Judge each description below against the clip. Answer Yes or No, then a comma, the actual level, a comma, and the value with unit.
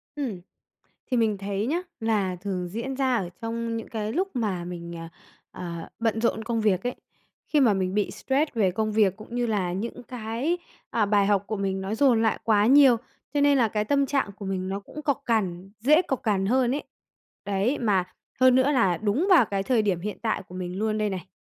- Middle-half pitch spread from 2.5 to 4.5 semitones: Yes, average, 4.2 semitones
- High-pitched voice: Yes, high, 215 Hz